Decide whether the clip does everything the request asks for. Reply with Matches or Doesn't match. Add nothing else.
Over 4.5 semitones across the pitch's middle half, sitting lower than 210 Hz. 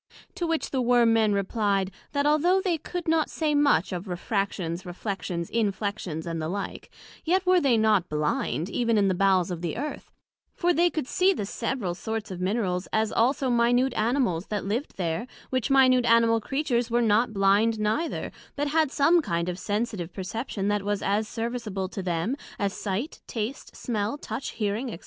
Doesn't match